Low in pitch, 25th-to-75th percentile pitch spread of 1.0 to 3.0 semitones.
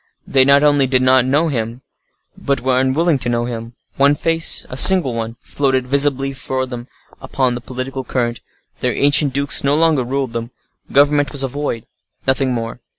Yes: low, 130 Hz; narrow, 2.4 semitones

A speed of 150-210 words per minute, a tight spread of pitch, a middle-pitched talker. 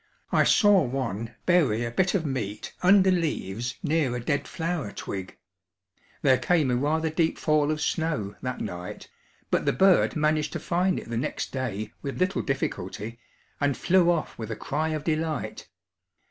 No: average, 170 wpm; wide, 5.6 semitones; medium, 150 Hz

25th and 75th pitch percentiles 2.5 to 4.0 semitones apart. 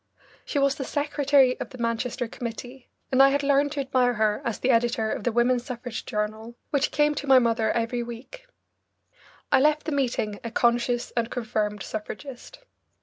Yes: average, 3.0 semitones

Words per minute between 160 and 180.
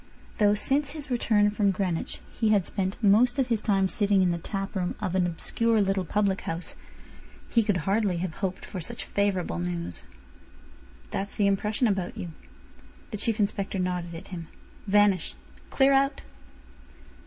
Yes: average, 165 wpm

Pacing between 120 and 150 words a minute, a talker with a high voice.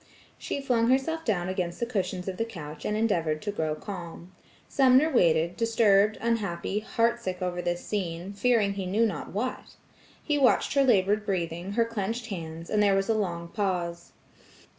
No: average, 170 wpm; high, 200 Hz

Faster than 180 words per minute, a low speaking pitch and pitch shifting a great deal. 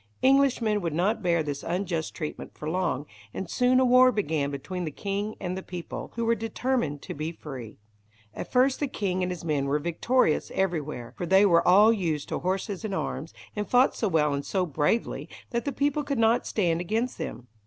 No: fast, 205 wpm; medium, 185 Hz; wide, 6.3 semitones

